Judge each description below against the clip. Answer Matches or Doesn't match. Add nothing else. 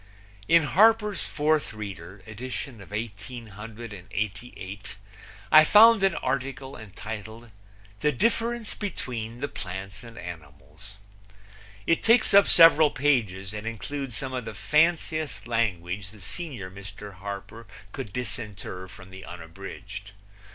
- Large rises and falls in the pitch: Matches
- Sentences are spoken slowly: Matches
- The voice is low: Matches